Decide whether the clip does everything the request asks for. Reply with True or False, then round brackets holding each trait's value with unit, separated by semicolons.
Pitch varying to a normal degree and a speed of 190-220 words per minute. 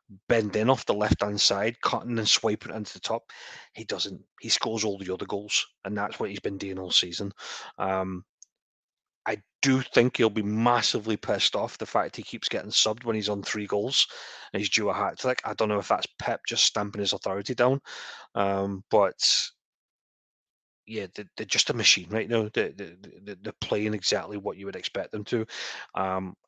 False (2.3 semitones; 195 wpm)